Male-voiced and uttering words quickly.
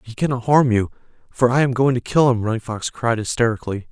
Yes: male; fast, 230 wpm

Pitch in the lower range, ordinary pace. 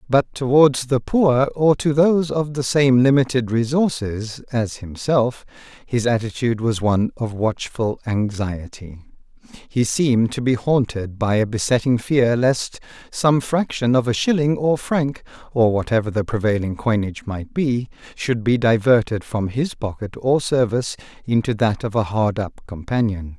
Yes: low, 120 Hz; average, 155 wpm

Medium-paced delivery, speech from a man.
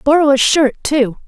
No: average, 190 wpm; female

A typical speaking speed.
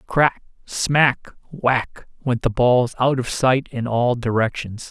No: slow, 120 wpm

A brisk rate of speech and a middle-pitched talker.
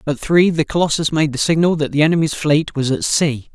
Yes: fast, 235 wpm; medium, 150 Hz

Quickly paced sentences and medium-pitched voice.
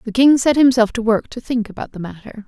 No: fast, 265 wpm; high, 230 Hz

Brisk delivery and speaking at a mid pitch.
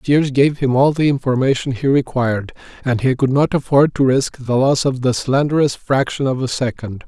No: fast, 210 wpm; low, 130 Hz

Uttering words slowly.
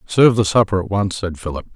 No: fast, 240 wpm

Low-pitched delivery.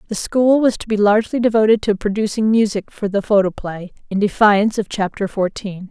No: high, 210 Hz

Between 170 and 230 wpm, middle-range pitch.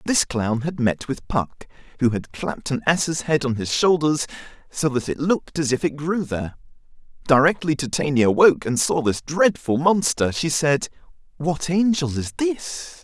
Yes: average, 175 wpm; medium, 145 Hz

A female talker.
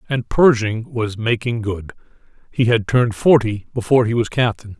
No: male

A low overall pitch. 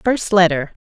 No: medium, 185 Hz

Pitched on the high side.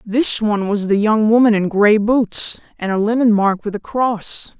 Yes: high, 215 Hz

